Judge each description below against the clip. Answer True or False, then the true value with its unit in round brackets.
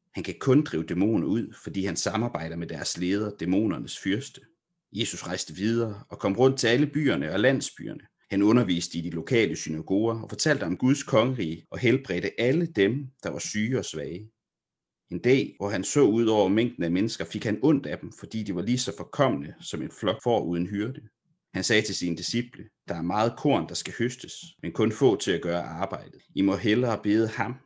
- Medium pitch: False (110 Hz)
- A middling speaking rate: True (210 wpm)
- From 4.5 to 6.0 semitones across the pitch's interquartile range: True (5.2 semitones)